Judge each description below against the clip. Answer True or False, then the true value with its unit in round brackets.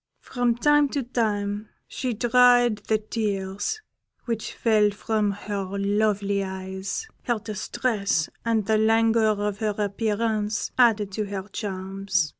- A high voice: True (210 Hz)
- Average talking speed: False (125 wpm)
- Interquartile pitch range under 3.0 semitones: True (2.4 semitones)